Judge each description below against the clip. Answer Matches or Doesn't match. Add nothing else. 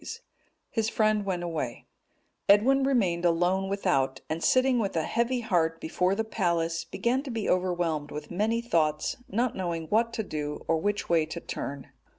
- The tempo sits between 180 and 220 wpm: Doesn't match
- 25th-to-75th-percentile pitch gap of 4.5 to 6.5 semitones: Matches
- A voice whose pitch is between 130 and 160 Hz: Doesn't match